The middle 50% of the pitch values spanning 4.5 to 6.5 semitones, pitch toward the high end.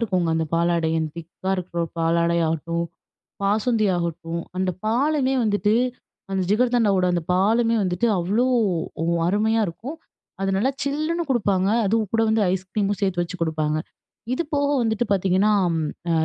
Yes: average, 4.9 semitones; high, 195 Hz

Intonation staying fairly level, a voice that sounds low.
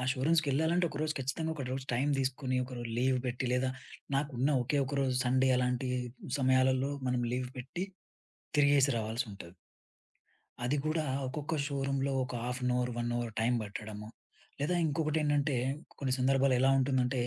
Yes: narrow, 2.3 semitones; low, 130 Hz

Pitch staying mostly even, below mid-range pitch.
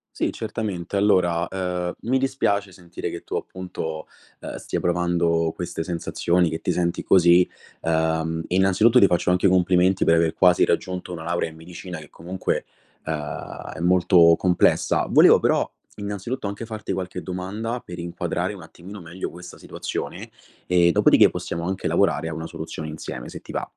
Yes: narrow, 2.1 semitones; very low, 90 Hz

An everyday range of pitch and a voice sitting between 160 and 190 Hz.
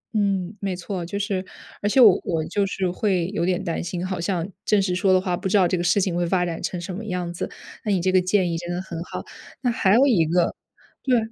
No: narrow, 2.3 semitones; medium, 185 Hz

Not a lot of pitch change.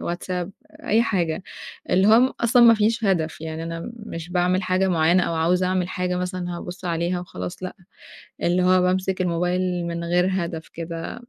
Yes: narrow, 1.6 semitones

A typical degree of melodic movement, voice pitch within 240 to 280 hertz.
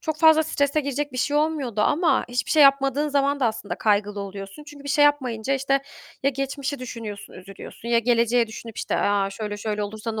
Yes: average, 4.9 semitones; very high, 255 Hz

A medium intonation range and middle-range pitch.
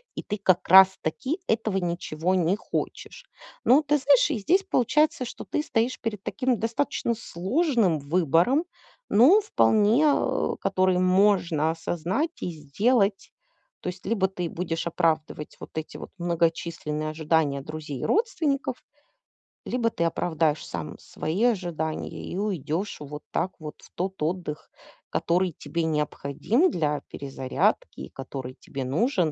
No: wide, 6.5 semitones; medium, 180 Hz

